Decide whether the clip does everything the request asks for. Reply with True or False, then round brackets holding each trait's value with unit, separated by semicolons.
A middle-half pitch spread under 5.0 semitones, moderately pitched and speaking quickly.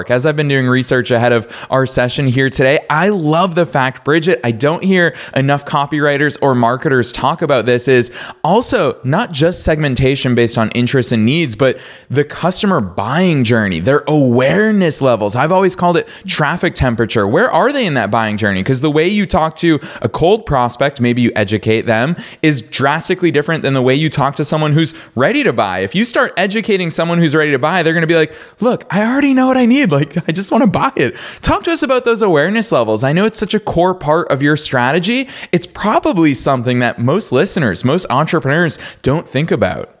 False (5.6 semitones; 150 Hz; 210 wpm)